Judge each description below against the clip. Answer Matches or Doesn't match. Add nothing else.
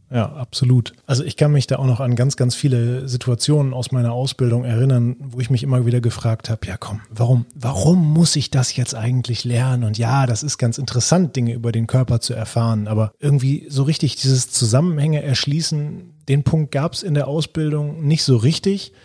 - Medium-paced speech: Doesn't match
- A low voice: Matches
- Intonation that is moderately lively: Matches